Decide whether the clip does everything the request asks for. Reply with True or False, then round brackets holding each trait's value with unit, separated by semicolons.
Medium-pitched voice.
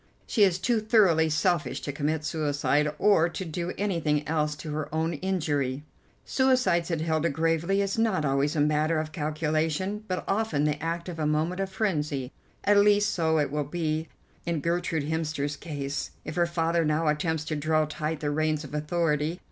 True (160 Hz)